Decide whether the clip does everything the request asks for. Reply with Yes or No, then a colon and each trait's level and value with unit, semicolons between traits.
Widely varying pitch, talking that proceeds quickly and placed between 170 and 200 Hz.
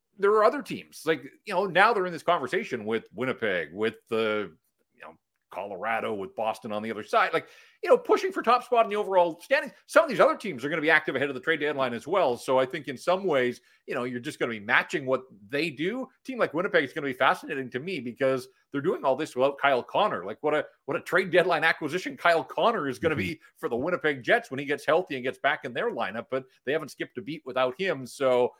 No: wide, 6.4 semitones; fast, 265 wpm; medium, 150 Hz